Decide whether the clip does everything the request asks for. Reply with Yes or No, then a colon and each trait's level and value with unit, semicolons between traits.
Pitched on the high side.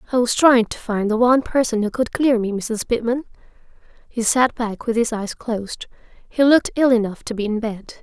Yes: high, 230 Hz